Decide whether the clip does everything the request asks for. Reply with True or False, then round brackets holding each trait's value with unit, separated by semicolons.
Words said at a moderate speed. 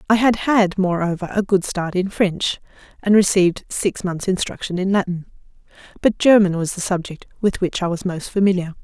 True (185 wpm)